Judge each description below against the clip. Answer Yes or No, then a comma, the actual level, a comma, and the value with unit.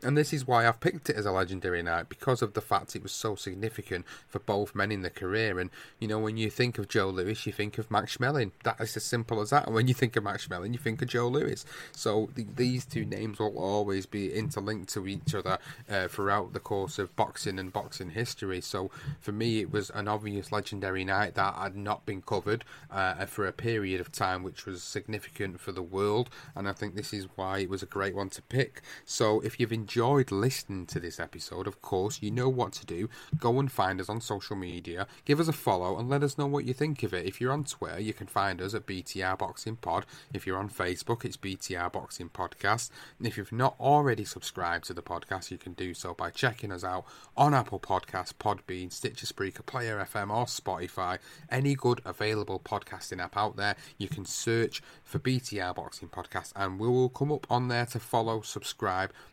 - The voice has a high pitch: No, low, 105 Hz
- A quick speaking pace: Yes, fast, 225 wpm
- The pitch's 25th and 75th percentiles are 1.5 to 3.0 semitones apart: No, average, 4.1 semitones